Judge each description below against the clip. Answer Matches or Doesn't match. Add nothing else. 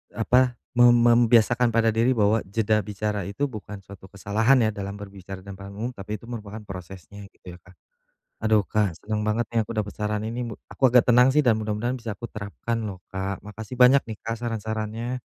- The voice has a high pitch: Doesn't match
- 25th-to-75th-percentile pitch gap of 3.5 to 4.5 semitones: Doesn't match